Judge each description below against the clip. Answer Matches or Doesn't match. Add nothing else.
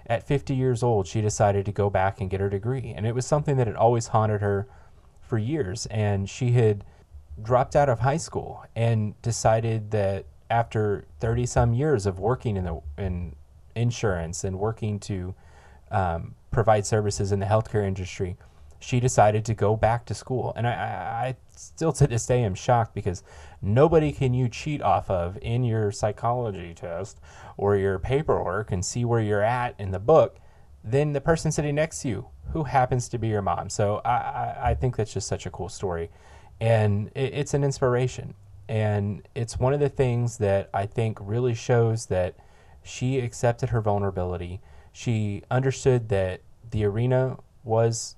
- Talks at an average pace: Matches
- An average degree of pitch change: Matches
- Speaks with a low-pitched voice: Matches